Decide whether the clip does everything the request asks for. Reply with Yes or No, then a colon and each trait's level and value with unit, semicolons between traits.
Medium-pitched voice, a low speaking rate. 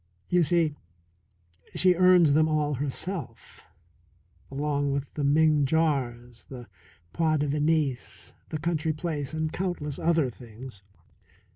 Yes: medium, 150 Hz; slow, 120 wpm